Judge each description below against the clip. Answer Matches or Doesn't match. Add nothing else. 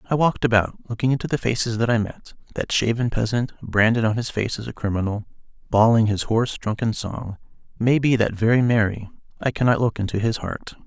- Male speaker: Matches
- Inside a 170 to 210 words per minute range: Matches